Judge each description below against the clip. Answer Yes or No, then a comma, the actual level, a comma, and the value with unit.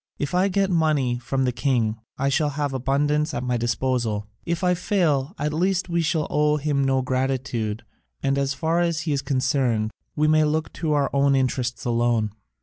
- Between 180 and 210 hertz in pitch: No, medium, 140 Hz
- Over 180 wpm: Yes, average, 190 wpm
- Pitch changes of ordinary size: Yes, average, 3.5 semitones